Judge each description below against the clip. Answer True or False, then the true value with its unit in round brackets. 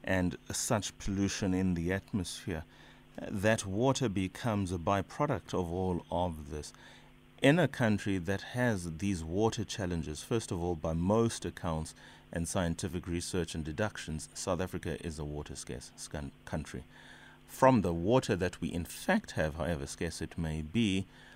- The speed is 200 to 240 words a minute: False (155 wpm)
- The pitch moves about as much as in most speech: True (3.9 semitones)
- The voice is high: False (90 Hz)